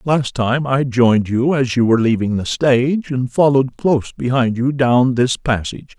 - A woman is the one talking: No, male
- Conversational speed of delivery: Yes, average, 190 wpm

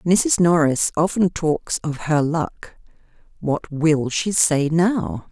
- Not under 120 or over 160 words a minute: Yes, slow, 135 wpm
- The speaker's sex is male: No, female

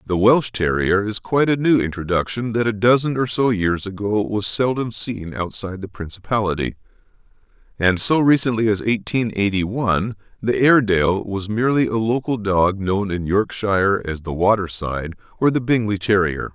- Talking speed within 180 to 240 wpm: No, average, 165 wpm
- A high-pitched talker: No, low, 105 Hz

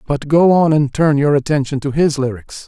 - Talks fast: Yes, fast, 225 wpm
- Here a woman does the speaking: No, male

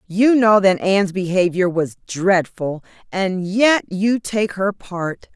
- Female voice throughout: Yes, female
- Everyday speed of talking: Yes, average, 145 wpm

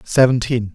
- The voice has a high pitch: No, low, 120 Hz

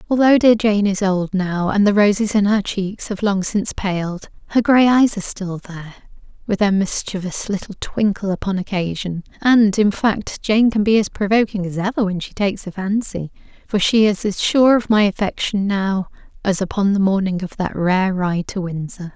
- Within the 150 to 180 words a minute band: No, average, 195 wpm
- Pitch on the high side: Yes, high, 200 Hz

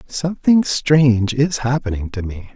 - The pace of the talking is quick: No, average, 140 wpm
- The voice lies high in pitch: No, low, 130 Hz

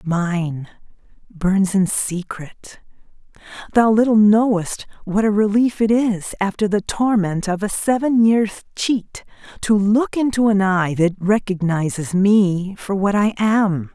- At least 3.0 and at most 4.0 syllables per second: Yes, 3.7 syllables/s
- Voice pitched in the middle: No, high, 200 Hz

